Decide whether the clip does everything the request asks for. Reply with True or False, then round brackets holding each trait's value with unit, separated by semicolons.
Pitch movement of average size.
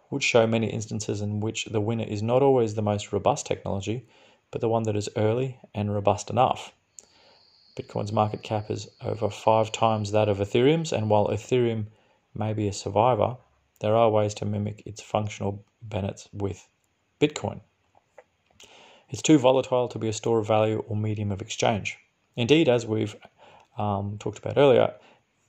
False (1.6 semitones)